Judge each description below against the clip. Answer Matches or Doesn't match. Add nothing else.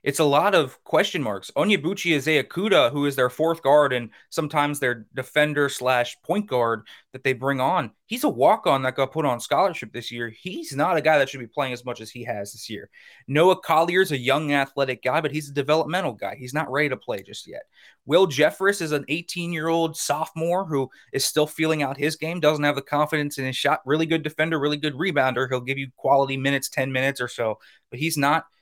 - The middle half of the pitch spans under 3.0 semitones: Doesn't match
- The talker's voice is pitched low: Doesn't match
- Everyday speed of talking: Doesn't match